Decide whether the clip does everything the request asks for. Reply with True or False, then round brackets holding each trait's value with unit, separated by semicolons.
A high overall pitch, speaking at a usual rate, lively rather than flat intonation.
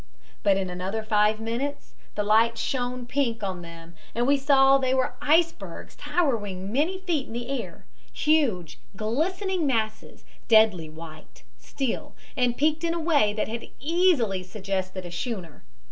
True (230 Hz; 150 wpm; 6.3 semitones)